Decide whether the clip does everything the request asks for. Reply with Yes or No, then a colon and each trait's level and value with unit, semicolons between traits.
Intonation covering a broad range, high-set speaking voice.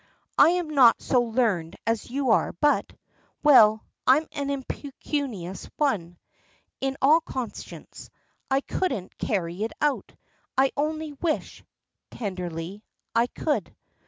Yes: wide, 5.7 semitones; very high, 255 Hz